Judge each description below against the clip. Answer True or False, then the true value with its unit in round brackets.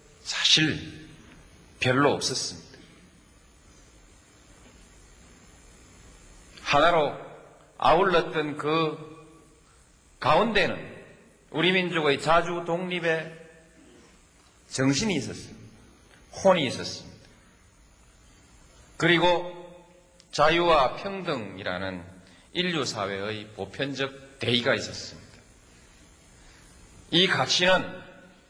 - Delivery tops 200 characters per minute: False (160 characters per minute)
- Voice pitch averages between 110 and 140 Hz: True (135 Hz)